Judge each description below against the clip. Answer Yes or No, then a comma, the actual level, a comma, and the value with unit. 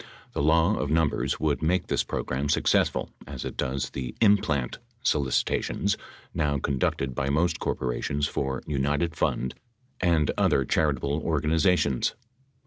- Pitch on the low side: Yes, very low, 75 Hz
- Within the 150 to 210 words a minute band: No, slow, 135 wpm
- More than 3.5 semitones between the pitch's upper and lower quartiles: No, average, 3.1 semitones